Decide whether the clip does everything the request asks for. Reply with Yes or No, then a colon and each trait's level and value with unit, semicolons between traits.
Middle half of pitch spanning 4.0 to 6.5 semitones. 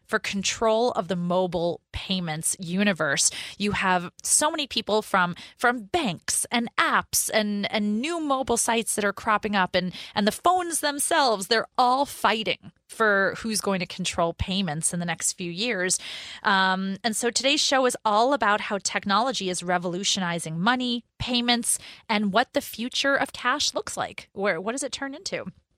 Yes: average, 4.7 semitones